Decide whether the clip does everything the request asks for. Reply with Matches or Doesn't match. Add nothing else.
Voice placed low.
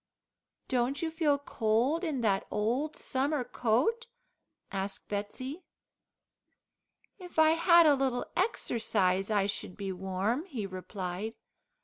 Doesn't match